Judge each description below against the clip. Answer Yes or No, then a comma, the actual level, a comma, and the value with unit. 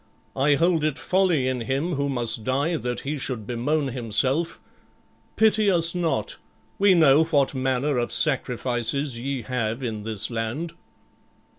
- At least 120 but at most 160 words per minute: Yes, average, 145 wpm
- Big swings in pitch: No, average, 4.8 semitones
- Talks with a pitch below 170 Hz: Yes, low, 135 Hz